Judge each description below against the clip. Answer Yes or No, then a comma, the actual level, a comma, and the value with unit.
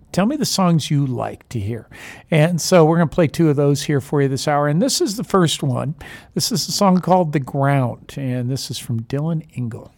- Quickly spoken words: Yes, fast, 245 wpm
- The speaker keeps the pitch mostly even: No, average, 4.4 semitones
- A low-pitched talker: No, medium, 145 Hz